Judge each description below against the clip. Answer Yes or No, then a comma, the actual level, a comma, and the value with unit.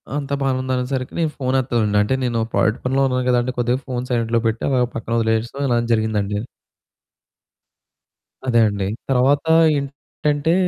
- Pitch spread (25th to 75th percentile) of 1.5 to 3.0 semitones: Yes, average, 2.7 semitones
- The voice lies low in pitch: Yes, low, 125 Hz